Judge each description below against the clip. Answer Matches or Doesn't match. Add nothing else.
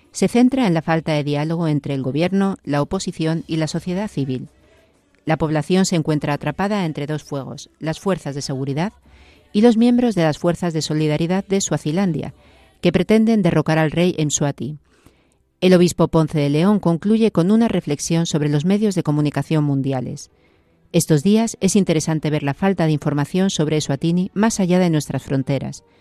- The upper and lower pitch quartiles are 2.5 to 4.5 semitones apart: Matches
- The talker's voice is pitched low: Doesn't match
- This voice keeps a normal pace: Matches